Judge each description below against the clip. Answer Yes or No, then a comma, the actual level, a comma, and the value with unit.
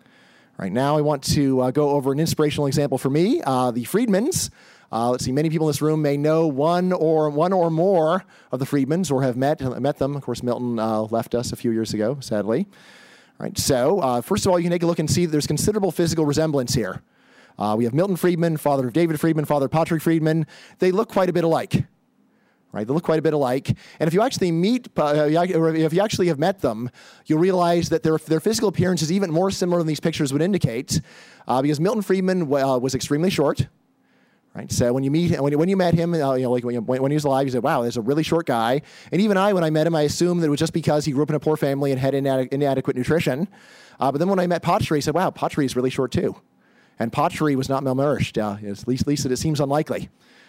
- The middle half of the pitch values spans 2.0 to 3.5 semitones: No, average, 4.1 semitones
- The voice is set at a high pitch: No, medium, 150 Hz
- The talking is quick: Yes, fast, 260 wpm